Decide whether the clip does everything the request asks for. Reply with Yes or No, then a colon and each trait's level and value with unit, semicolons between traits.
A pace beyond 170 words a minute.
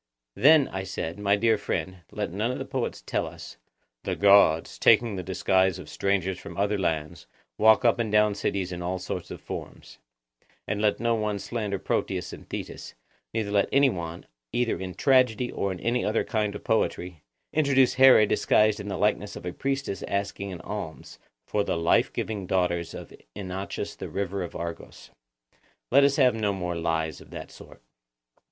Yes: average, 185 wpm